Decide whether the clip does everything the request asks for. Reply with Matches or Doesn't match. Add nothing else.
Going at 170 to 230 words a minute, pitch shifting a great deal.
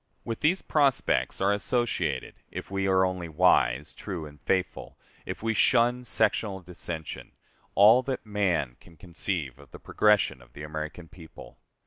Doesn't match